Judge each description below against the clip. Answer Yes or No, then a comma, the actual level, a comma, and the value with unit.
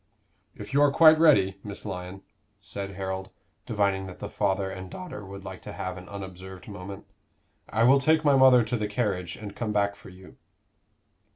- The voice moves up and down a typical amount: Yes, average, 4.1 semitones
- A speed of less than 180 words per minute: No, average, 185 wpm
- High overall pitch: No, low, 100 Hz